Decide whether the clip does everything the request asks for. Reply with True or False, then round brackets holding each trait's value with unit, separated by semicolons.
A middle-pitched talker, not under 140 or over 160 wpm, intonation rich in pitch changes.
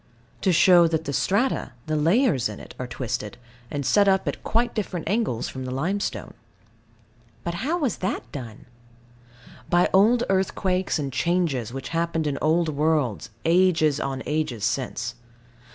True (160 Hz; 150 wpm; 5.8 semitones)